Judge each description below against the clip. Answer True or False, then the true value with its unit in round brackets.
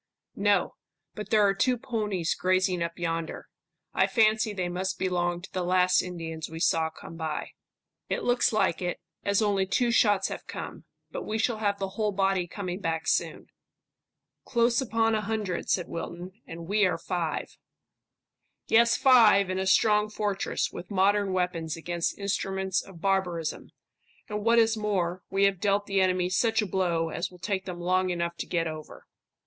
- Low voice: False (190 Hz)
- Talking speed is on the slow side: False (175 wpm)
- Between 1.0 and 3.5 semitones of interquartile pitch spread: True (3.0 semitones)